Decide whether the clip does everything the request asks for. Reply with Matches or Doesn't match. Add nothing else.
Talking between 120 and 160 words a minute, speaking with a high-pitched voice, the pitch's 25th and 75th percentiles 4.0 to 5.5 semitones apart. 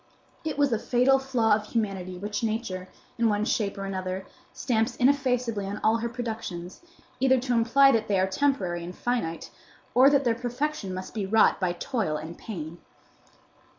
Doesn't match